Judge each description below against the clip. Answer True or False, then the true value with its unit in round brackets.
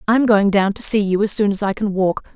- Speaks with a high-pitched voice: True (205 Hz)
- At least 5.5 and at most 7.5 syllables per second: True (5.8 syllables/s)